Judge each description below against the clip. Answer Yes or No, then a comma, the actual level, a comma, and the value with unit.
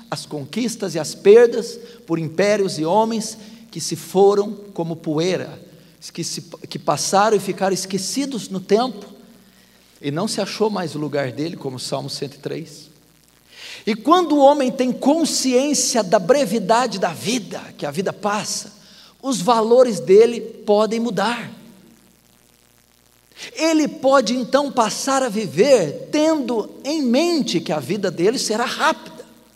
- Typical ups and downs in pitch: No, wide, 6.2 semitones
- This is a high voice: Yes, high, 215 Hz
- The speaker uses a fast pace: No, average, 140 wpm